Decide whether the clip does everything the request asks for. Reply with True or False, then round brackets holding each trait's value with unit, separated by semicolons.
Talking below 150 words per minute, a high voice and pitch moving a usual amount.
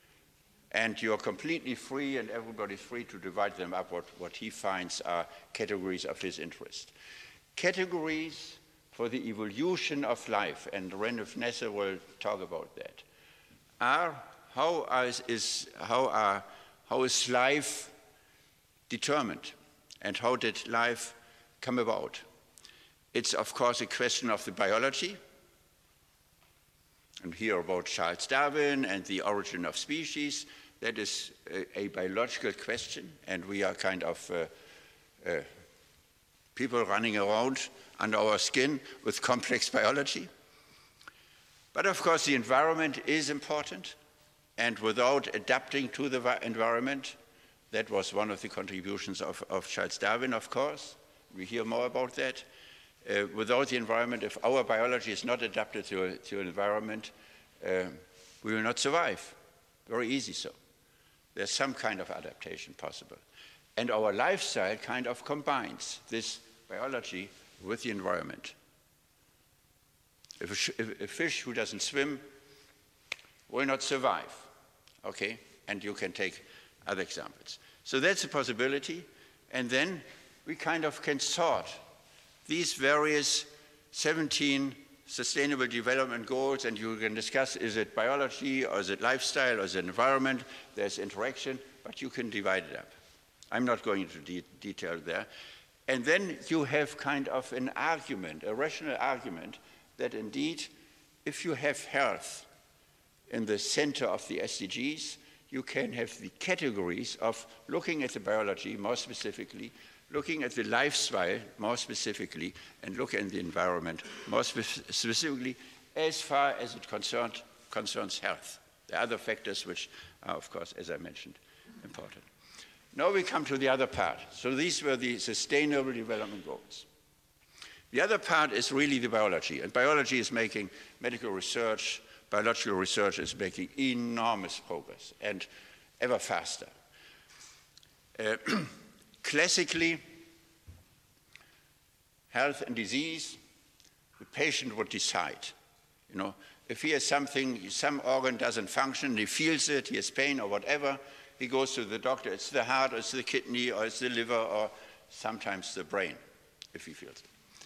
False (140 wpm; 130 Hz; 4.5 semitones)